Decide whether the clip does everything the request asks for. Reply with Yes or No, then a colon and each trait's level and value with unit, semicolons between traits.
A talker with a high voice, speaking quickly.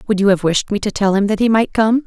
Yes: high, 210 Hz; fast, 350 wpm